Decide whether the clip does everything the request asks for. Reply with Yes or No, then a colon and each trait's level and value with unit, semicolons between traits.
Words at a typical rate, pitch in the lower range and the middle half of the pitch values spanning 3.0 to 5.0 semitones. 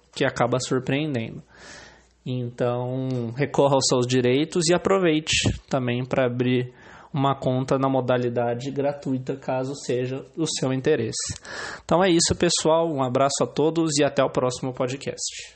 No: average, 140 wpm; low, 130 Hz; narrow, 2.4 semitones